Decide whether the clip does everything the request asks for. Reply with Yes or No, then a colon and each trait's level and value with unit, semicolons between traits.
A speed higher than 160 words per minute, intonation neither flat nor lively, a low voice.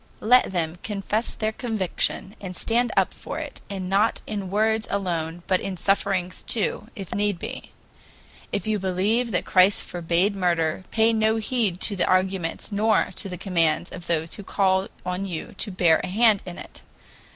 No: average, 175 wpm; average, 3.1 semitones; high, 195 Hz